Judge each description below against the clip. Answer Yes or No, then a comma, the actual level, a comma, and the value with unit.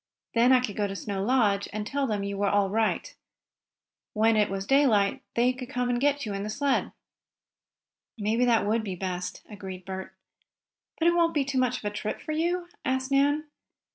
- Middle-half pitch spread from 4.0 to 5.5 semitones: Yes, average, 5.0 semitones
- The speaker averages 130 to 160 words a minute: No, average, 200 wpm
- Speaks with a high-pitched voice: Yes, high, 225 Hz